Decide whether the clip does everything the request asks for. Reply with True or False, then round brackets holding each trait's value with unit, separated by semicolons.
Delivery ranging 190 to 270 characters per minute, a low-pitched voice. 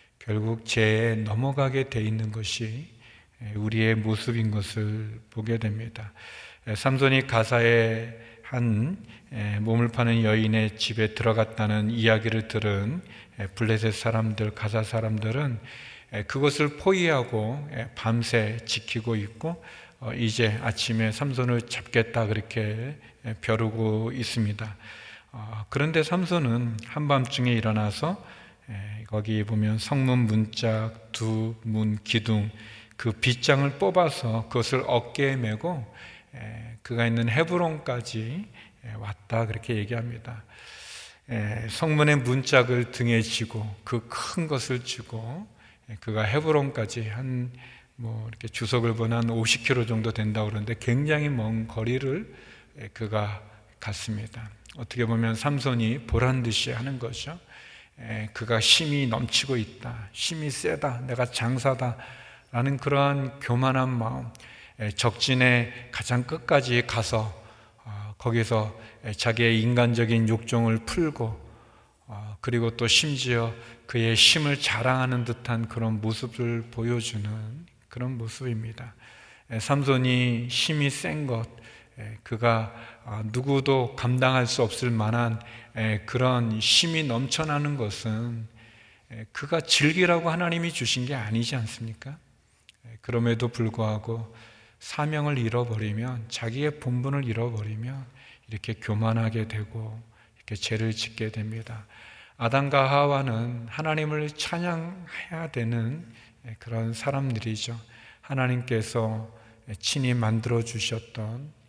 True (240 characters per minute; 115 Hz)